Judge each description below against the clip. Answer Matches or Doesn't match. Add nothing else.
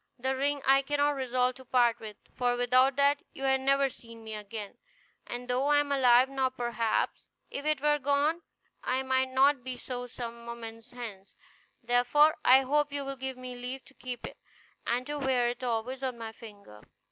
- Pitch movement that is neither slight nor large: Doesn't match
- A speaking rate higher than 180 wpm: Matches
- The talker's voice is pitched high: Matches